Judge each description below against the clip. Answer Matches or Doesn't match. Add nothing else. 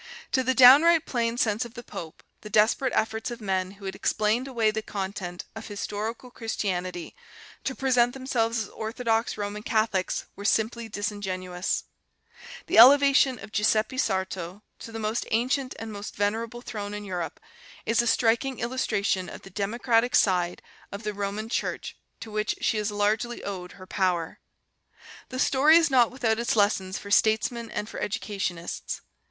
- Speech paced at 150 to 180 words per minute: Matches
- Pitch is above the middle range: Matches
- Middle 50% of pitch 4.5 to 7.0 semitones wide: Doesn't match